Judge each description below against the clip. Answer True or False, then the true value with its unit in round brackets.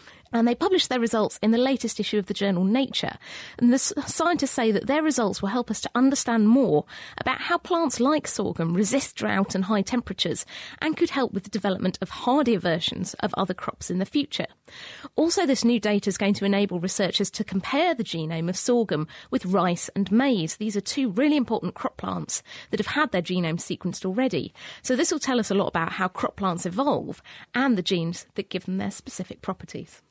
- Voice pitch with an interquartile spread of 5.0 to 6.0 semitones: True (5.6 semitones)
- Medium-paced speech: False (210 wpm)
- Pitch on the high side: True (215 Hz)